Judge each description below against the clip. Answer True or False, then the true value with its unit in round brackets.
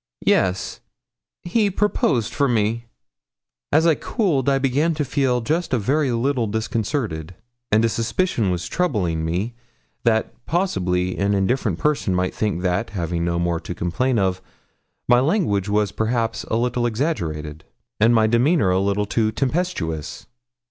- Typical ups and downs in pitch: False (6.6 semitones)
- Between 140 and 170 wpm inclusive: True (150 wpm)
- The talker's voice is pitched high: False (110 Hz)